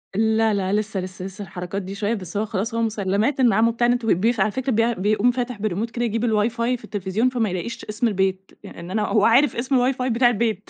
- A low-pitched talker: No, high, 220 Hz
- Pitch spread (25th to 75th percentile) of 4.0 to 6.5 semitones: No, average, 3.1 semitones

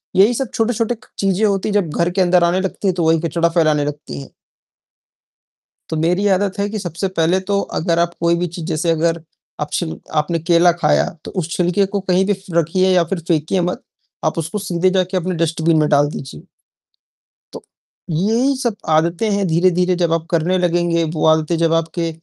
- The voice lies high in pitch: No, medium, 175 Hz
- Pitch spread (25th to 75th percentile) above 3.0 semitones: No, narrow, 2.6 semitones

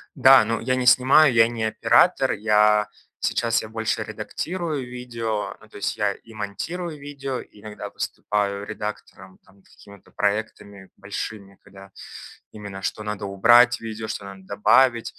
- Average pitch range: Yes, average, 3.2 semitones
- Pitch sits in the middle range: No, low, 110 Hz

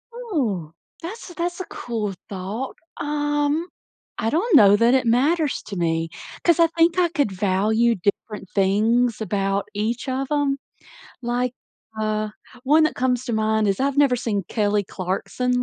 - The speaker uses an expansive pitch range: Yes, wide, 6.1 semitones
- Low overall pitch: No, high, 240 Hz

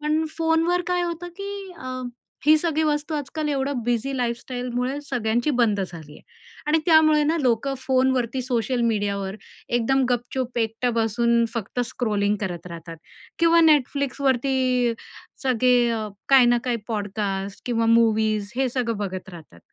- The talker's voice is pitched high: Yes, high, 245 Hz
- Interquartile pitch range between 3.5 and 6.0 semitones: Yes, average, 3.9 semitones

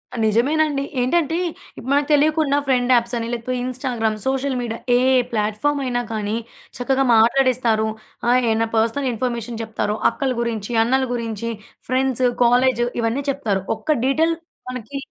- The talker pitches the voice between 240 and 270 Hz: Yes, high, 245 Hz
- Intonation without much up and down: No, average, 3.1 semitones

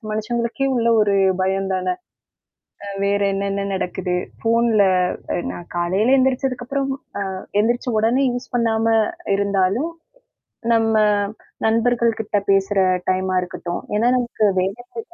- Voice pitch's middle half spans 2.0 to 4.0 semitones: Yes, average, 3.7 semitones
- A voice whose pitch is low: No, high, 220 Hz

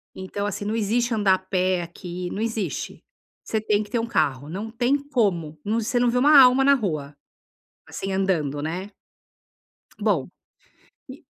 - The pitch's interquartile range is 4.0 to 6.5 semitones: Yes, average, 4.5 semitones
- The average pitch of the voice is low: No, high, 205 Hz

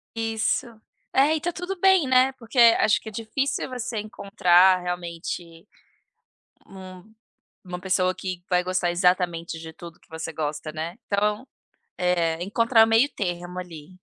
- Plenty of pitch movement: No, average, 4.5 semitones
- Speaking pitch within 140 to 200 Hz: Yes, medium, 185 Hz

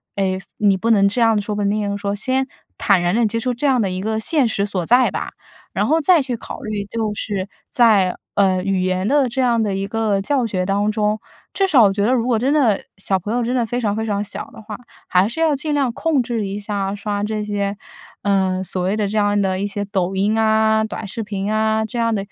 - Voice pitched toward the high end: Yes, high, 210 Hz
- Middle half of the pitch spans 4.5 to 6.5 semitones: No, average, 2.7 semitones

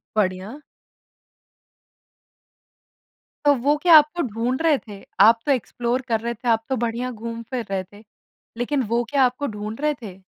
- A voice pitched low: No, high, 235 Hz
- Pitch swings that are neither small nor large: Yes, average, 3.7 semitones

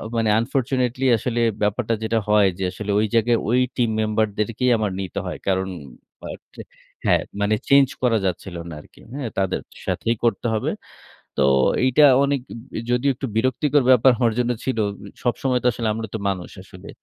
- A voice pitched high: No, low, 115 Hz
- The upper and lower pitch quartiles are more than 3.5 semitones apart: No, average, 3.2 semitones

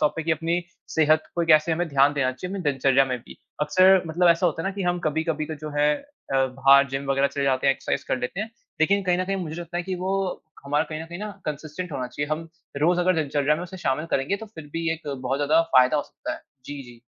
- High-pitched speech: No, medium, 155 Hz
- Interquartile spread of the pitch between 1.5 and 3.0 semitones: No, average, 4.0 semitones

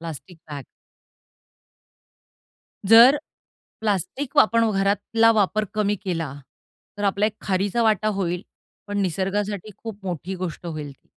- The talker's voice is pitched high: Yes, high, 200 Hz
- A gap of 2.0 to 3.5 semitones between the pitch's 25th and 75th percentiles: Yes, average, 3.1 semitones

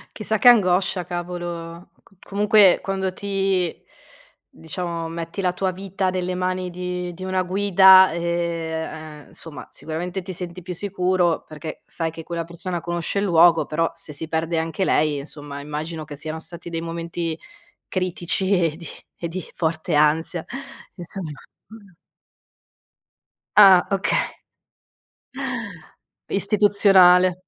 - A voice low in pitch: No, medium, 175 Hz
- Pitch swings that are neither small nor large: No, narrow, 2.3 semitones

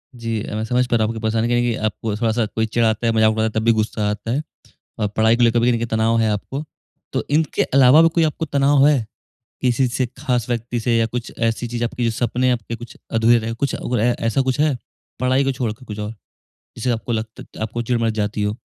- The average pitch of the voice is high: No, low, 115 Hz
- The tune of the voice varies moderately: No, narrow, 2.1 semitones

